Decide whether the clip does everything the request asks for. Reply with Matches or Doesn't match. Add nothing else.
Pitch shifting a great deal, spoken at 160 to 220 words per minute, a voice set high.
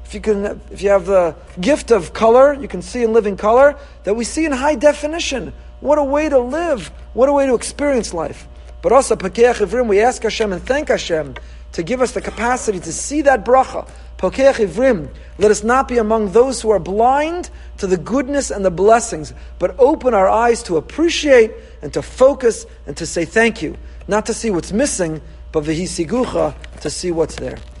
Matches